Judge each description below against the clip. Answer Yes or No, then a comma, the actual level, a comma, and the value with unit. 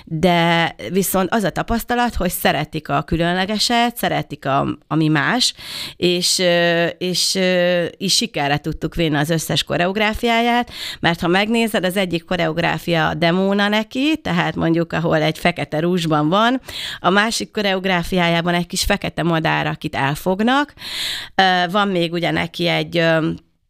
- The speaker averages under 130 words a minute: No, average, 135 wpm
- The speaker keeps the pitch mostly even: No, average, 3.4 semitones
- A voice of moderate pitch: Yes, medium, 175 Hz